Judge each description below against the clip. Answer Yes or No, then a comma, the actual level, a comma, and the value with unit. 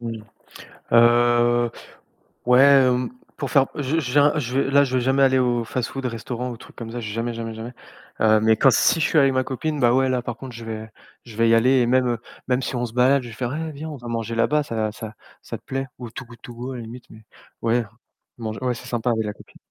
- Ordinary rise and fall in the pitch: No, narrow, 2.3 semitones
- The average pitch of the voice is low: Yes, low, 120 Hz